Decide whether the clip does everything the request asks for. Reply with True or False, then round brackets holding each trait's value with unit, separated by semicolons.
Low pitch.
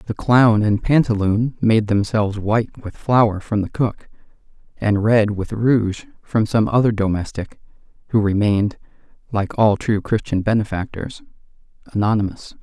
True (105 Hz)